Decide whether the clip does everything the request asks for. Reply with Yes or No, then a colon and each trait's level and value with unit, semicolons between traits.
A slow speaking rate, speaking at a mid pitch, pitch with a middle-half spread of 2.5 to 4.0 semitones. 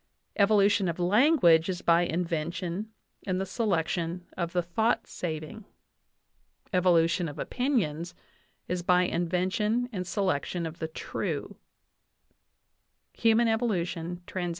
Yes: slow, 110 wpm; medium, 180 Hz; average, 3.4 semitones